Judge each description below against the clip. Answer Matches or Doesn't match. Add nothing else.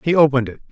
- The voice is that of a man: Matches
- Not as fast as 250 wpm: Doesn't match